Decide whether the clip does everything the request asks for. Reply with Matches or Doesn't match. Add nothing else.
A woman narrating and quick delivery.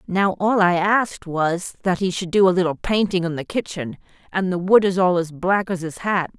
Matches